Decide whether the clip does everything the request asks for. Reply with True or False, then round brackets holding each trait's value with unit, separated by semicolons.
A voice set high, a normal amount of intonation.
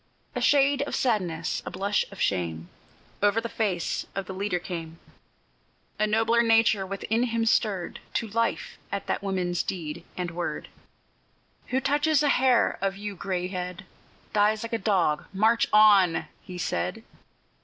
True (200 Hz; 4.1 semitones)